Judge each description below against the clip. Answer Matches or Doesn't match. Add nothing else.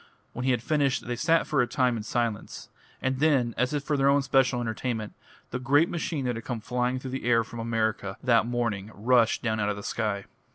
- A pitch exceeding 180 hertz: Doesn't match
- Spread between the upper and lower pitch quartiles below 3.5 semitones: Matches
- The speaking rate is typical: Doesn't match